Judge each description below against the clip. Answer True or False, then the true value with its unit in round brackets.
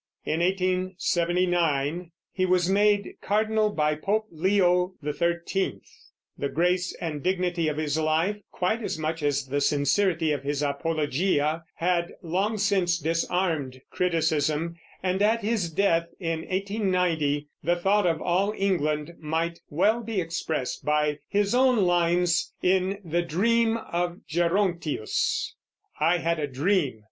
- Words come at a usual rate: False (130 wpm)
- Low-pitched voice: False (175 Hz)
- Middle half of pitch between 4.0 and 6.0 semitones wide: False (3.4 semitones)